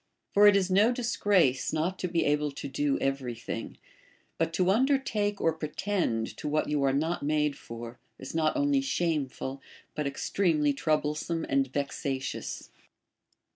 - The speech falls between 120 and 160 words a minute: Yes, average, 155 wpm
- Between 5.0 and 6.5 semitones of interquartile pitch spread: Yes, wide, 5.4 semitones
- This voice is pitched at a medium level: Yes, medium, 155 Hz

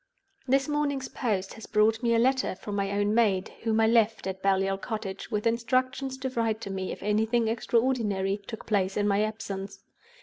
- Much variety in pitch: No, average, 3.1 semitones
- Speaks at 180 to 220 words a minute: Yes, average, 190 wpm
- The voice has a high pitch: Yes, high, 220 Hz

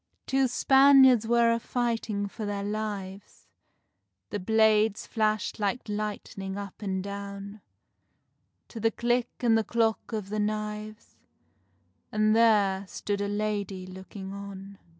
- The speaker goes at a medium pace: No, slow, 130 wpm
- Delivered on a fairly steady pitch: Yes, narrow, 2.0 semitones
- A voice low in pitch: No, high, 210 Hz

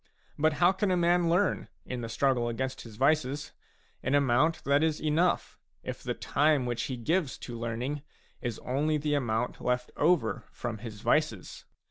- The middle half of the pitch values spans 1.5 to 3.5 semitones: No, average, 4.4 semitones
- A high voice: No, medium, 140 Hz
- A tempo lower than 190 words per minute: Yes, average, 170 wpm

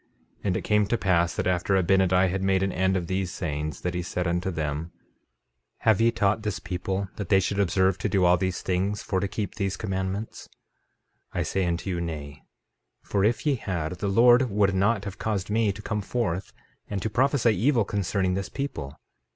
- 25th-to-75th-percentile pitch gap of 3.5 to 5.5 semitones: No, average, 2.7 semitones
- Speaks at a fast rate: Yes, fast, 210 wpm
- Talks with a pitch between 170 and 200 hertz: No, very low, 95 Hz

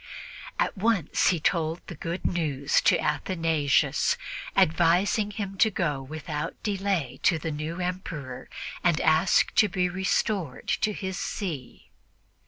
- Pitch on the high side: No, medium, 170 Hz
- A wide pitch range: No, average, 3.8 semitones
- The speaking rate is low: Yes, slow, 130 wpm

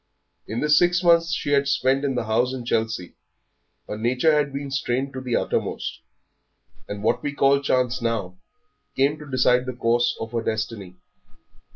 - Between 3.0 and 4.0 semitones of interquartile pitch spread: Yes, average, 3.4 semitones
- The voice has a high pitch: No, low, 125 Hz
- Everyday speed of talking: Yes, average, 175 wpm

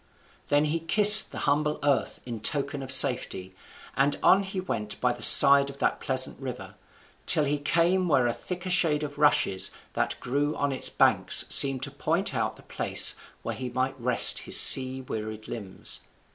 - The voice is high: No, medium, 140 Hz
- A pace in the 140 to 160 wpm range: No, average, 180 wpm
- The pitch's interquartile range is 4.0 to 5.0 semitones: No, average, 3.2 semitones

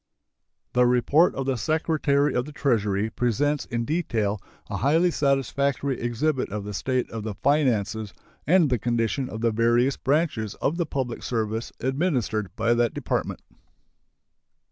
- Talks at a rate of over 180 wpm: No, average, 145 wpm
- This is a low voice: Yes, low, 125 Hz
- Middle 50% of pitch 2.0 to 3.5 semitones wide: No, average, 4.1 semitones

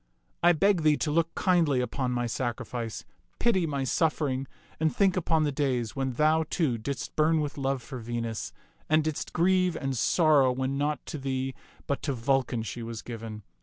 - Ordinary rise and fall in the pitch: Yes, average, 4.1 semitones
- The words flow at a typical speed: Yes, average, 180 wpm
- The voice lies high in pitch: No, medium, 140 Hz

